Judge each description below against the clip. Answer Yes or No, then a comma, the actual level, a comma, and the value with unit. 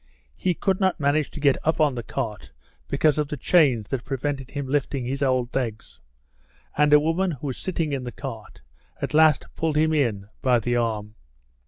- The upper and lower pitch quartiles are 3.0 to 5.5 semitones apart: Yes, average, 3.8 semitones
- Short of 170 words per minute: No, average, 195 wpm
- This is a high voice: No, medium, 140 Hz